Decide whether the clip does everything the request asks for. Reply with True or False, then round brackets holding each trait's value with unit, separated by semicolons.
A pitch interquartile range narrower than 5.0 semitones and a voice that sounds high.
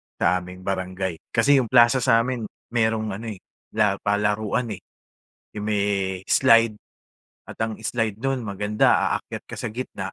False (2.6 semitones; 110 Hz)